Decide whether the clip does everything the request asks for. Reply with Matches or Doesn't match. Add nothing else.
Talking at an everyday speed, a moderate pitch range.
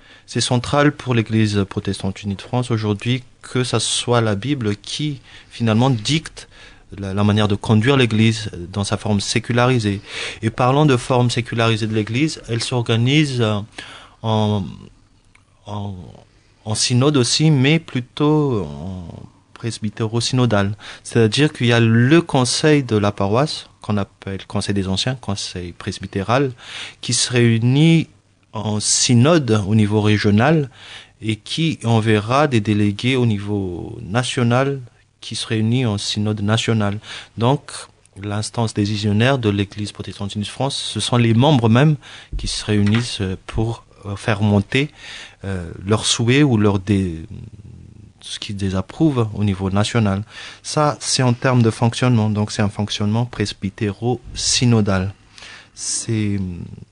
Doesn't match